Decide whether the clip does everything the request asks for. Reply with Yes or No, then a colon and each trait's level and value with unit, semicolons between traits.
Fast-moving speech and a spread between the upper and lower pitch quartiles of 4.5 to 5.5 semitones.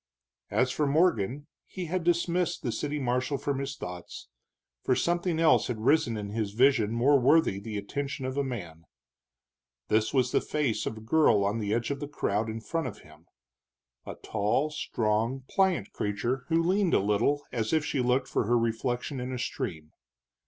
No: average, 185 wpm; average, 5.2 semitones